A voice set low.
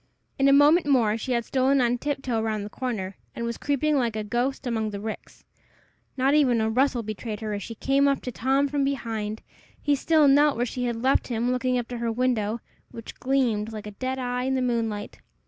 No: high, 245 Hz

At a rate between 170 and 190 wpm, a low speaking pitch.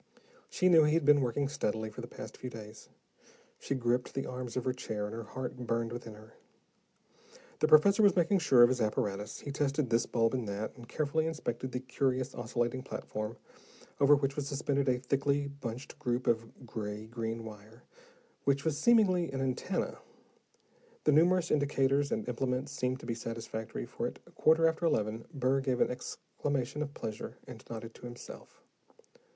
Yes: average, 180 wpm; low, 130 Hz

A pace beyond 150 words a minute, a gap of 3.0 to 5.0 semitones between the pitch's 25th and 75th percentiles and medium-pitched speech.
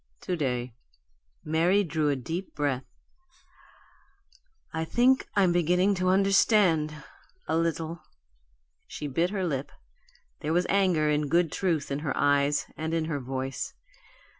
No: slow, 135 wpm; average, 3.7 semitones; medium, 160 Hz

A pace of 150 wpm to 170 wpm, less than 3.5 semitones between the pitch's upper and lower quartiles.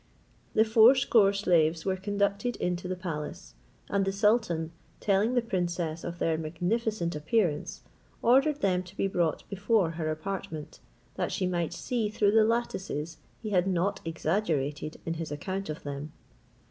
No: average, 155 wpm; average, 4.3 semitones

